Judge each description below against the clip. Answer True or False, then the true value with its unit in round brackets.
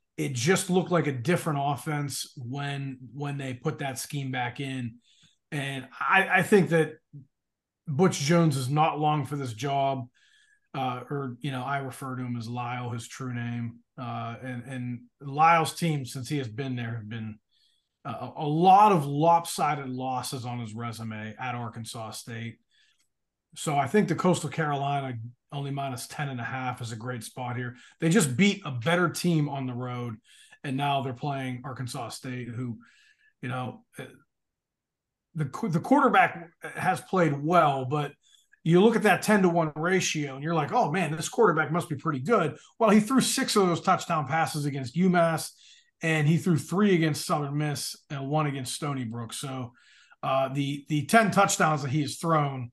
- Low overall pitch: False (145 Hz)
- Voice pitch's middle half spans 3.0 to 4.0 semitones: False (4.6 semitones)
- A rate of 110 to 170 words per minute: False (180 wpm)